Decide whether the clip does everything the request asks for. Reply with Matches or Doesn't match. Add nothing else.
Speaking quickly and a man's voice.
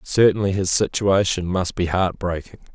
Doesn't match